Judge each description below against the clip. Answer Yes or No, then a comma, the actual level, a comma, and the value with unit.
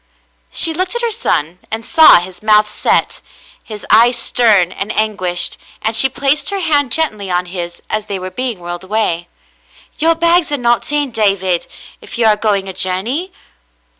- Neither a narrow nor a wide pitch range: No, wide, 7.4 semitones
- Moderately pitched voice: No, high, 215 Hz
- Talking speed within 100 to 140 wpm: No, average, 175 wpm